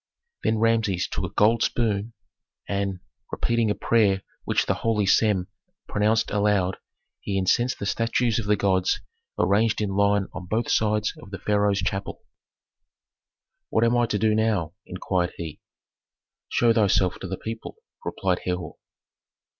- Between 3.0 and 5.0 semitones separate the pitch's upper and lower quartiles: No, narrow, 2.6 semitones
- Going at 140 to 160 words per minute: Yes, average, 145 wpm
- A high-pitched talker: No, low, 105 Hz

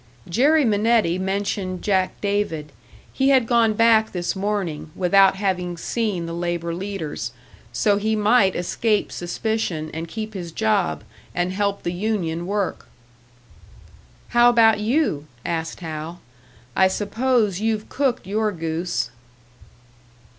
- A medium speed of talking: No, slow, 125 wpm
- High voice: Yes, high, 195 Hz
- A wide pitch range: No, average, 4.1 semitones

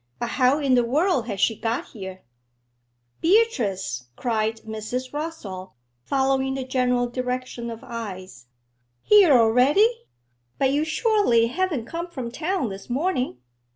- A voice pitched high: Yes, very high, 250 Hz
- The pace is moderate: No, slow, 130 wpm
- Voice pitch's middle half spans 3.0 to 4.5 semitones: No, average, 5.3 semitones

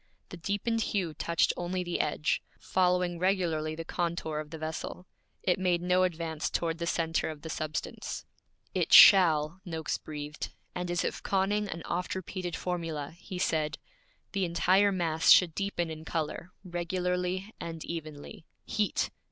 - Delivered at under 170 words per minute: Yes, average, 150 wpm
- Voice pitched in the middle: Yes, medium, 175 Hz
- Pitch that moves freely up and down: No, narrow, 2.4 semitones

